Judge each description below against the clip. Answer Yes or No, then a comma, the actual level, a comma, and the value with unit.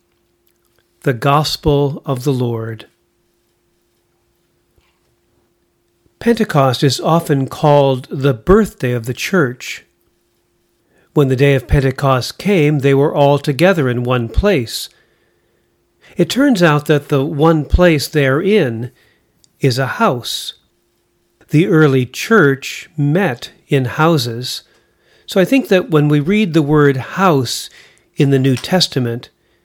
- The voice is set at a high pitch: No, medium, 140 Hz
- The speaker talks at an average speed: No, slow, 120 wpm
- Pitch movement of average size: Yes, average, 4.6 semitones